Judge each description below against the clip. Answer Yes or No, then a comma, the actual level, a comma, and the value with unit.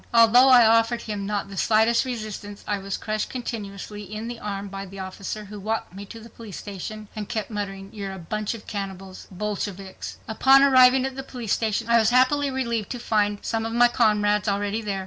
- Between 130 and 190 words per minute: No, average, 200 wpm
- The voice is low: No, high, 215 Hz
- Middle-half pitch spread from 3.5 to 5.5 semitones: No, average, 2.7 semitones